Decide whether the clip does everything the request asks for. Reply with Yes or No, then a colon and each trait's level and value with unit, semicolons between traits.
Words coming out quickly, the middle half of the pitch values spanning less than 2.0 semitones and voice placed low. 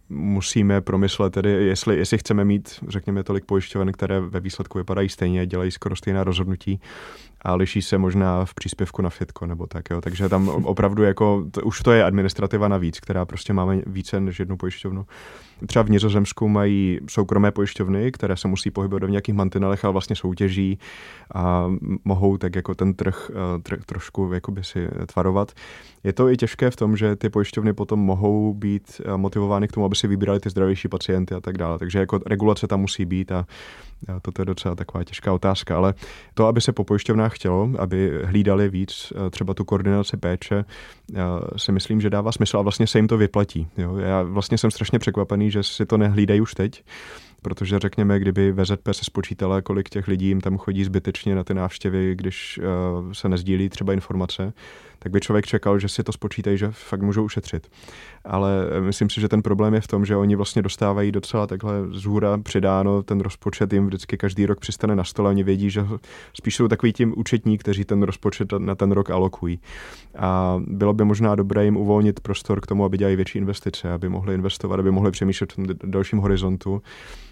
Yes: fast, 190 wpm; narrow, 1.4 semitones; low, 100 Hz